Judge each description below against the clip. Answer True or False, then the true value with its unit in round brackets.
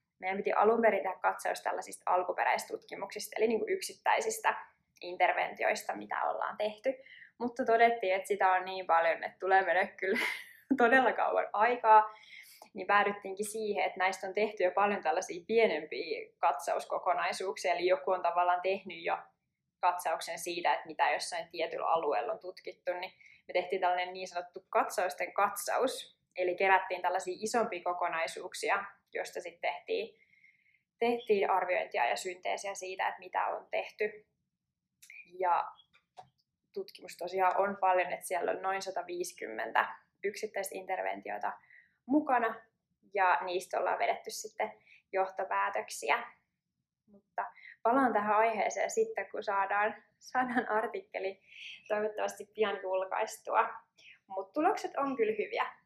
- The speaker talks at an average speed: True (125 wpm)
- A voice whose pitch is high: True (200 Hz)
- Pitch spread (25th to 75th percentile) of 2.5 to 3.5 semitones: False (3.9 semitones)